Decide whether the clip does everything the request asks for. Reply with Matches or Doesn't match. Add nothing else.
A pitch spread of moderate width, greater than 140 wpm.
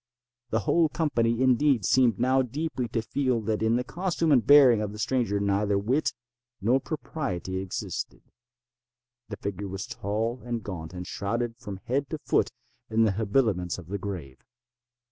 Matches